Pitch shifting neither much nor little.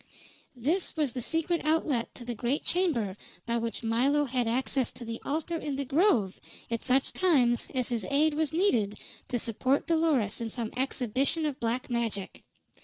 Yes: average, 4.6 semitones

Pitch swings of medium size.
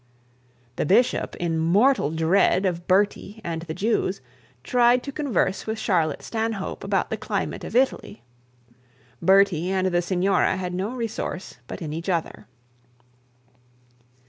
Yes: average, 4.5 semitones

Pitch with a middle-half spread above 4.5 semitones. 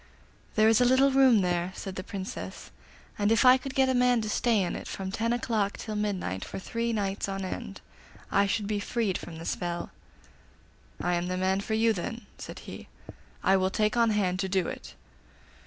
No: average, 3.5 semitones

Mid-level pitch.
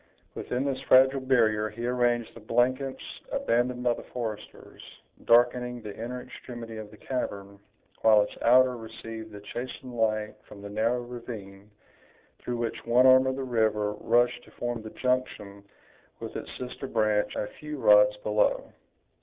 No: low, 120 Hz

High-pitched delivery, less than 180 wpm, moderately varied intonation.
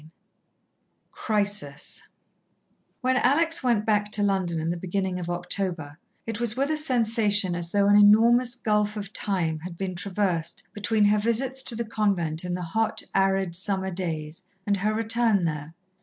Yes: high, 200 Hz; average, 165 wpm; average, 4.0 semitones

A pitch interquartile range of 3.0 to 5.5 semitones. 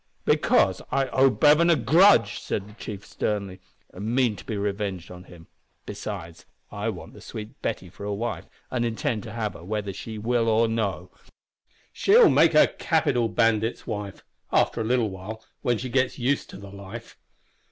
Yes: average, 3.4 semitones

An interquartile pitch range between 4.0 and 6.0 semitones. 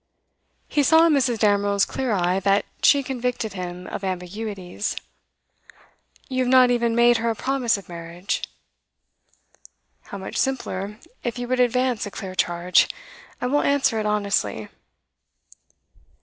Yes: average, 4.8 semitones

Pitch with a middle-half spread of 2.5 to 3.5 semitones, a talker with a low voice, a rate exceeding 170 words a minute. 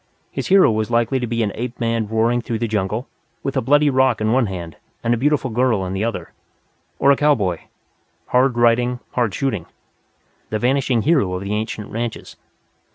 Yes: average, 3.1 semitones; low, 115 Hz; average, 190 wpm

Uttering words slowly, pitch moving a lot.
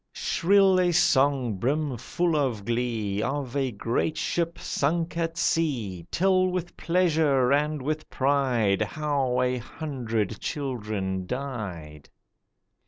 Yes: slow, 115 wpm; wide, 5.7 semitones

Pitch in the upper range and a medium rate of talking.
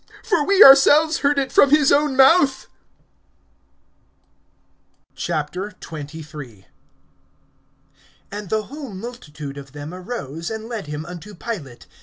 No: high, 210 Hz; slow, 110 wpm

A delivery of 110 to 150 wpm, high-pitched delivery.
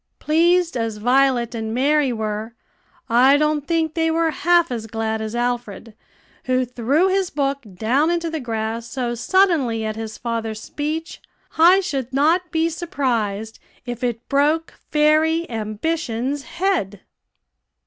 Yes: average, 140 wpm; very high, 265 Hz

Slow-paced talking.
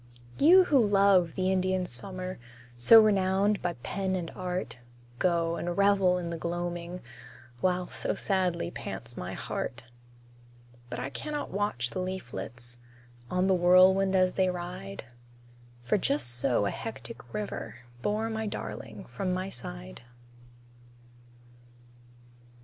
Yes: slow, 130 wpm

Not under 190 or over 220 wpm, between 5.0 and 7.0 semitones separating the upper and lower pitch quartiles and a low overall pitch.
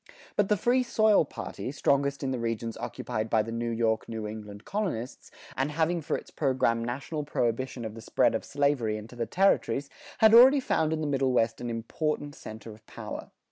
Yes: average, 195 wpm; average, 5.3 semitones; low, 130 Hz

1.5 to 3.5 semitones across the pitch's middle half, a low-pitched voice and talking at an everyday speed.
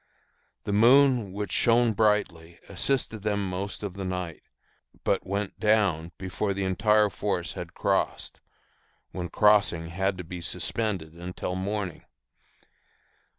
No: average, 2.7 semitones; low, 100 Hz; slow, 125 wpm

